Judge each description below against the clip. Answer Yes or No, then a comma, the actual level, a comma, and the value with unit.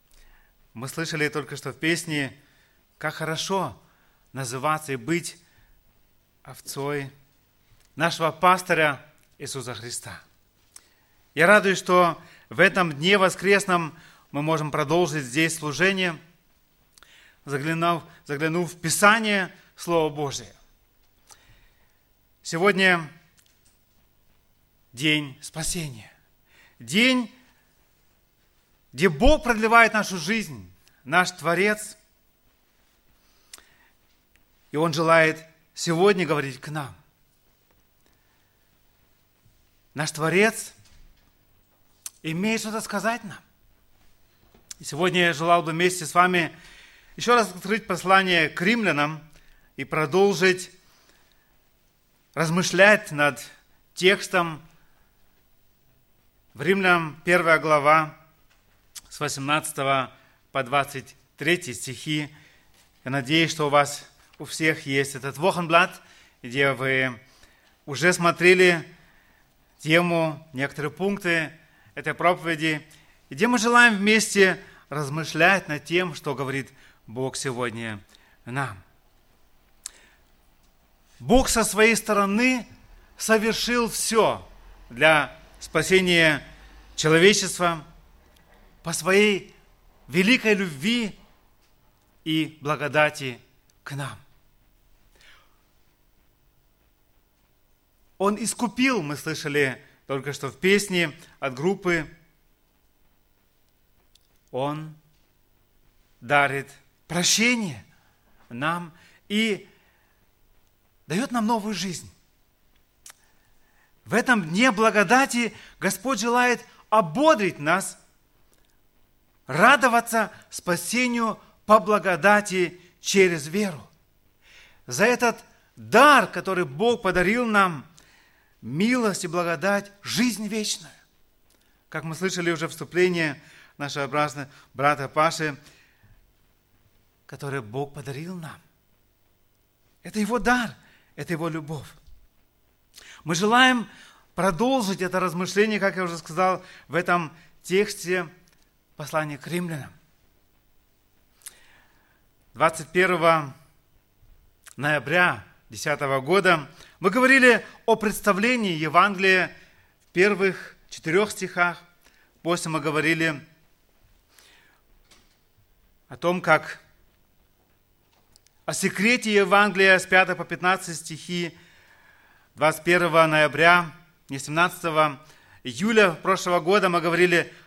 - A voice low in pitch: No, medium, 160 Hz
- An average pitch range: No, wide, 6.3 semitones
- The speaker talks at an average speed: No, slow, 85 wpm